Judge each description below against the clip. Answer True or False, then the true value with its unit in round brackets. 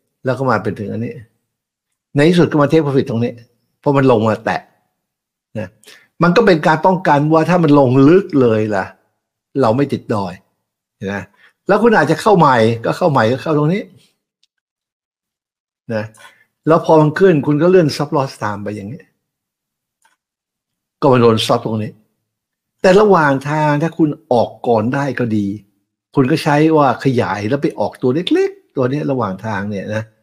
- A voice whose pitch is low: True (130 Hz)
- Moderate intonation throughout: False (6.1 semitones)